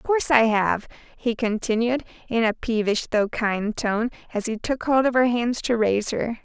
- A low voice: No, high, 230 Hz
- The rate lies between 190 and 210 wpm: Yes, fast, 205 wpm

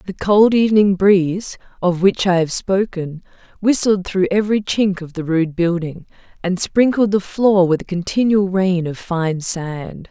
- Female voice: Yes, female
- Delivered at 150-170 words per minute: Yes, average, 165 wpm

